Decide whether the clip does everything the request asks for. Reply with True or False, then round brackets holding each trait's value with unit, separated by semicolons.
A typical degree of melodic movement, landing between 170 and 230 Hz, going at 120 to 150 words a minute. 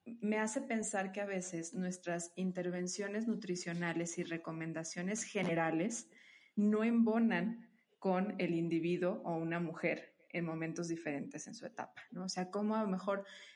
True (3.9 semitones; 185 Hz; 145 wpm)